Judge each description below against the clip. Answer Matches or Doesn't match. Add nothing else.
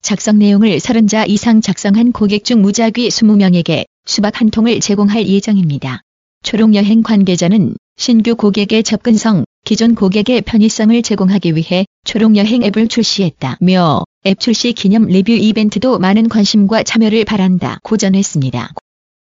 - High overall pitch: Matches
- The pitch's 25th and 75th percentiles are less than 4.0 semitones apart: Matches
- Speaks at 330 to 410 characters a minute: Doesn't match